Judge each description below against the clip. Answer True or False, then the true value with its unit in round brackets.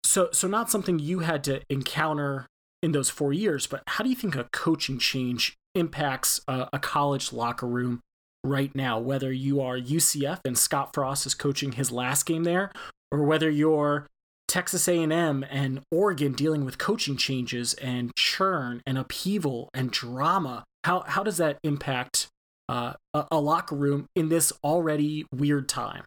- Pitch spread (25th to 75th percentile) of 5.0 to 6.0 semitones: False (3.5 semitones)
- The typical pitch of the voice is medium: True (145 Hz)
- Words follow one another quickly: False (170 wpm)